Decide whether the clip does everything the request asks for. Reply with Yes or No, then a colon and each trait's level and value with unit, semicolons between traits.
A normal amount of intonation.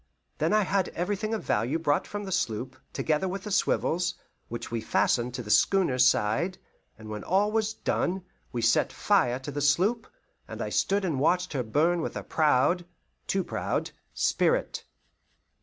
No: wide, 7.1 semitones